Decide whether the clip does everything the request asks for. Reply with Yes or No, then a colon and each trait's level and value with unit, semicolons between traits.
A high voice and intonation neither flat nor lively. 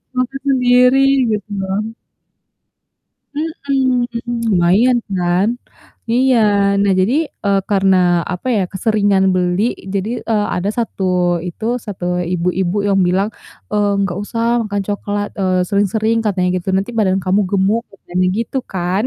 Yes: high, 200 Hz; average, 3.6 semitones